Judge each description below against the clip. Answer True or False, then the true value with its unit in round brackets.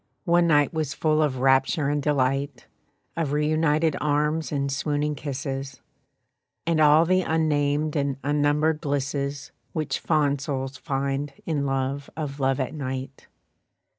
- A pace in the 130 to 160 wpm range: True (135 wpm)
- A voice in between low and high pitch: True (145 Hz)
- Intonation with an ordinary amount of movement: False (2.0 semitones)